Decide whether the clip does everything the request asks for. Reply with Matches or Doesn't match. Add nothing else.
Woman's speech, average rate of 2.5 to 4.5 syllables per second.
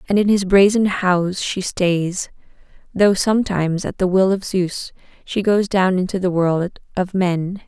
Matches